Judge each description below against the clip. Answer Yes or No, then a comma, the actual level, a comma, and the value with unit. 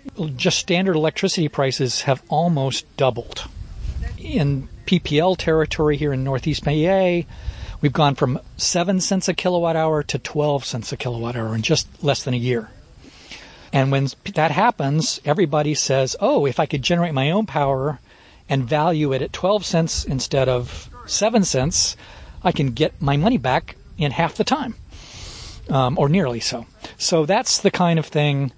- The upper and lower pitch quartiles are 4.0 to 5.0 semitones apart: Yes, average, 4.5 semitones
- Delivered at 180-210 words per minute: No, average, 165 wpm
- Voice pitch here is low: No, medium, 150 Hz